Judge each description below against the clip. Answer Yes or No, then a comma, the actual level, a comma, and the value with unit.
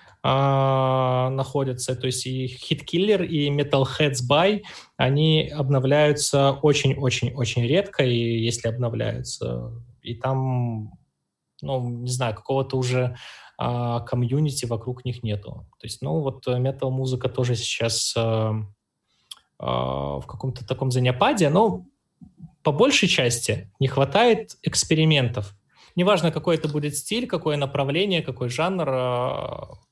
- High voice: No, low, 130 Hz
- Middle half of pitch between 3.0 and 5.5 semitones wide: Yes, average, 3.4 semitones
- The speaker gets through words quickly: No, average, 125 wpm